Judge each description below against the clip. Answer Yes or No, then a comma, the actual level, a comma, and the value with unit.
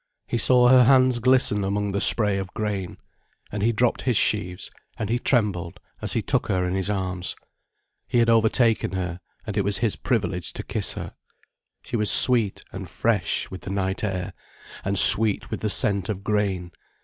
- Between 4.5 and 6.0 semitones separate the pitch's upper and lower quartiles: No, average, 3.4 semitones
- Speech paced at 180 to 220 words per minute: Yes, average, 190 wpm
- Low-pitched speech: Yes, low, 105 Hz